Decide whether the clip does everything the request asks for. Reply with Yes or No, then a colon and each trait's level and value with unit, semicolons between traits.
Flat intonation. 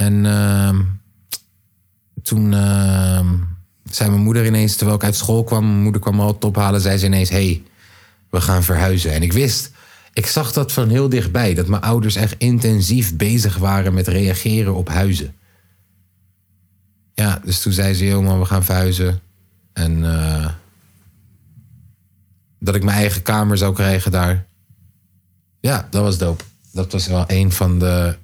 Yes: narrow, 2.1 semitones